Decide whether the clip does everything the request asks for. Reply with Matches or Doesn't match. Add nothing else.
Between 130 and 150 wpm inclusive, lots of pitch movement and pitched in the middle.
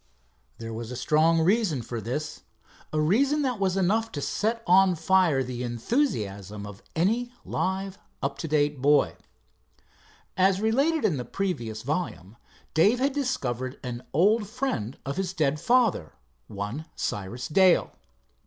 Matches